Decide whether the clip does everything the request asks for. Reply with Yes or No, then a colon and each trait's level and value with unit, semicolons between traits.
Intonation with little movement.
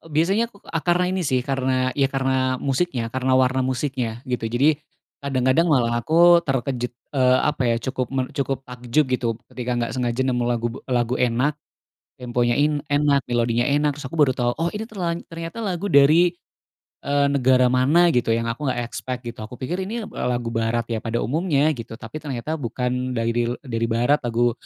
No: average, 3.4 semitones